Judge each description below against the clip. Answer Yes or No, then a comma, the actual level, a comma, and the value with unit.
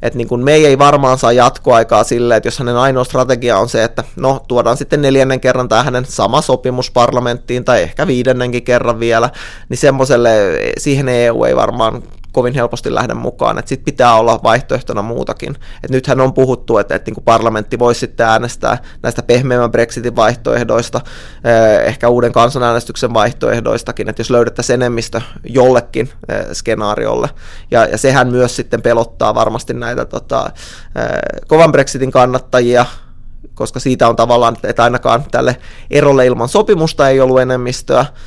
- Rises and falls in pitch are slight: Yes, narrow, 1.6 semitones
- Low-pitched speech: Yes, low, 125 Hz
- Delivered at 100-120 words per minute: No, average, 150 wpm